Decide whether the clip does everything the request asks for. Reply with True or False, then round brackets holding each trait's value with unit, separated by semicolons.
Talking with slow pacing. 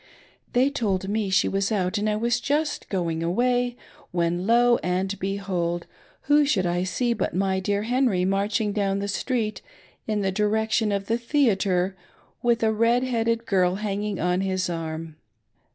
False (165 wpm)